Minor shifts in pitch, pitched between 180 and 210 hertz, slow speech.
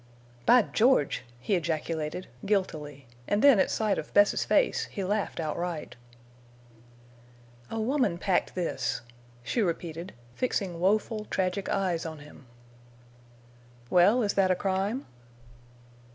No: average, 4.1 semitones; high, 190 Hz; slow, 120 wpm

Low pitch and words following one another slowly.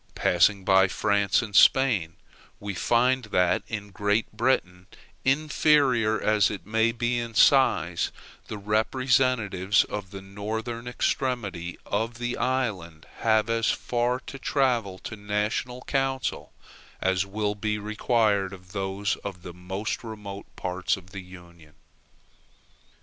Yes: low, 105 Hz; slow, 130 wpm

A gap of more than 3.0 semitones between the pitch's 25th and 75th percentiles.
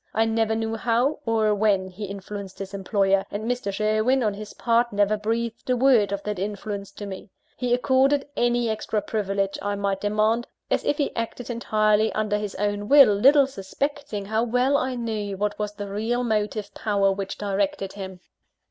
No: average, 2.7 semitones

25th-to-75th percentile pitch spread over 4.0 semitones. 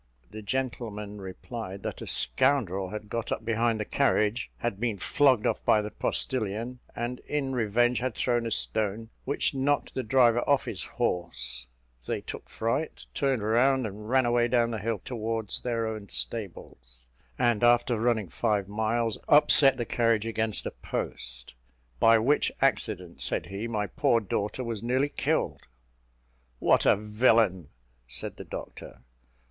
No: average, 2.8 semitones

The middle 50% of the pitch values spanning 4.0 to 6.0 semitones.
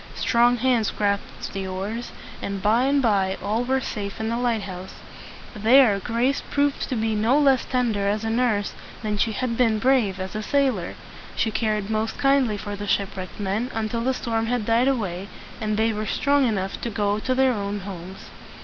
No: average, 3.4 semitones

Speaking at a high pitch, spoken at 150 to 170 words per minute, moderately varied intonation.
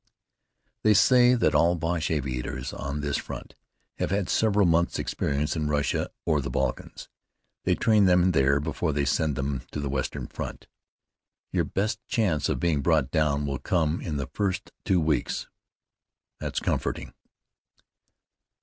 No: very low, 80 Hz; average, 155 wpm; average, 4.4 semitones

